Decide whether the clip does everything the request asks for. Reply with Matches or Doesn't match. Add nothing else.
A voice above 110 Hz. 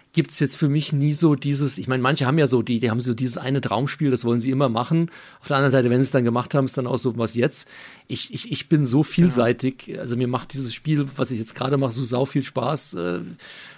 Matches